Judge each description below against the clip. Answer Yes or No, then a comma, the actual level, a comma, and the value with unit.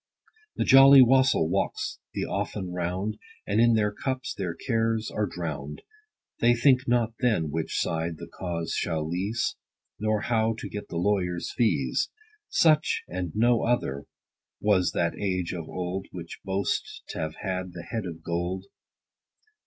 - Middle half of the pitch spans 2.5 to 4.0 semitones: No, average, 4.9 semitones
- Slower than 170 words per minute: Yes, average, 155 wpm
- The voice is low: Yes, very low, 95 Hz